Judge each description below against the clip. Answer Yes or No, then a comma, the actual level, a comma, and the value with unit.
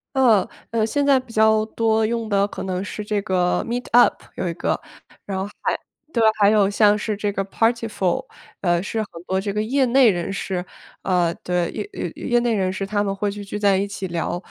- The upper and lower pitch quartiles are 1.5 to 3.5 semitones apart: Yes, average, 2.9 semitones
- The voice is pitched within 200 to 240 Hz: Yes, high, 205 Hz